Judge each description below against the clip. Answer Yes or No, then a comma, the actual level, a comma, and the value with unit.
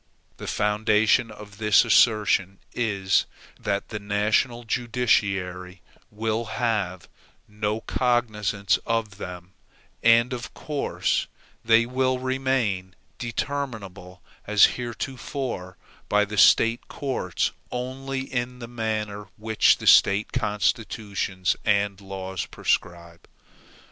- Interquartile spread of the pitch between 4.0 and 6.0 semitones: No, average, 3.4 semitones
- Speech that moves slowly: Yes, slow, 105 wpm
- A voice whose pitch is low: Yes, low, 105 Hz